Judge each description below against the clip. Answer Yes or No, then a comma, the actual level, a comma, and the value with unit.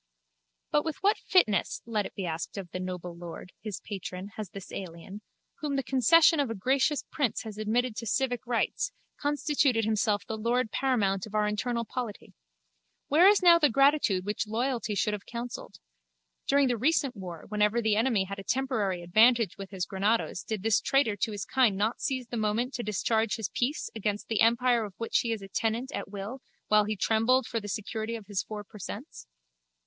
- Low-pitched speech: No, high, 220 Hz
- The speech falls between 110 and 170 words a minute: No, average, 195 wpm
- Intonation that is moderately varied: Yes, average, 3.8 semitones